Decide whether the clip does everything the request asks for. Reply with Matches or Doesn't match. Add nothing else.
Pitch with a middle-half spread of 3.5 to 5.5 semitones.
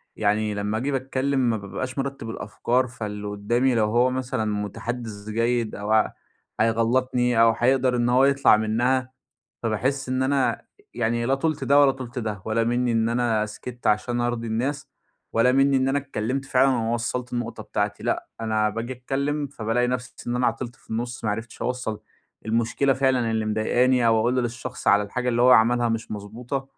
Doesn't match